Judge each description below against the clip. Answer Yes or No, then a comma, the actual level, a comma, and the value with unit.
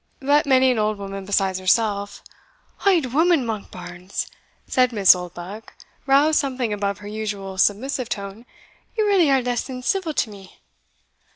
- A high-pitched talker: Yes, high, 220 Hz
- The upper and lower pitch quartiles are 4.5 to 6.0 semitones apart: Yes, average, 5.2 semitones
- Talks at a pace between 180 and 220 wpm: No, average, 150 wpm